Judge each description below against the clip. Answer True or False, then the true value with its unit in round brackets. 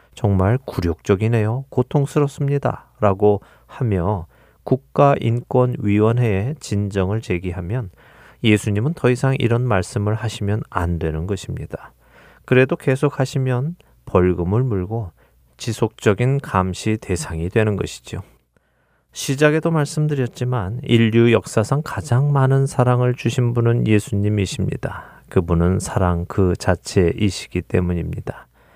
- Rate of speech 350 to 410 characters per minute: False (275 characters per minute)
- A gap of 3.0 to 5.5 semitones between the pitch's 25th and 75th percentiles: True (5.2 semitones)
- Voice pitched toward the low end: True (110 Hz)